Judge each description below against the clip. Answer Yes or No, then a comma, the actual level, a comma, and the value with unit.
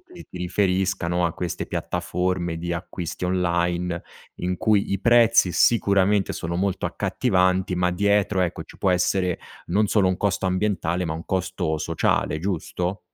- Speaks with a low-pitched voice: Yes, very low, 90 Hz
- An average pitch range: No, narrow, 2.0 semitones